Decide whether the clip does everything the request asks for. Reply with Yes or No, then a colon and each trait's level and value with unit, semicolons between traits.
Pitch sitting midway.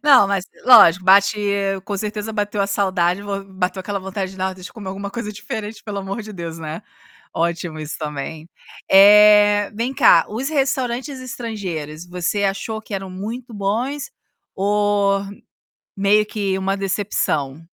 No: high, 200 Hz